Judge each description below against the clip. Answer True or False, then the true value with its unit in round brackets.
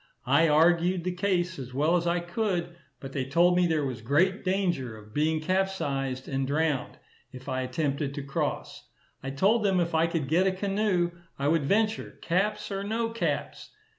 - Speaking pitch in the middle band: True (170 Hz)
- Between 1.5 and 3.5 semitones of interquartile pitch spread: False (5.1 semitones)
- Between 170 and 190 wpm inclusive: True (185 wpm)